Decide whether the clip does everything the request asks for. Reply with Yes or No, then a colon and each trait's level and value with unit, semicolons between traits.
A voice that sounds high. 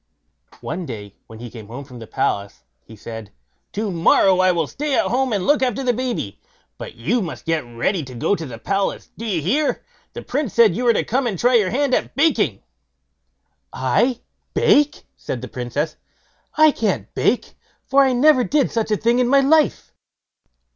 Yes: high, 205 Hz